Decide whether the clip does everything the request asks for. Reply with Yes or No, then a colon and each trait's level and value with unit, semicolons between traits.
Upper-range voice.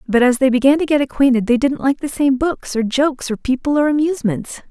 Yes: very high, 265 Hz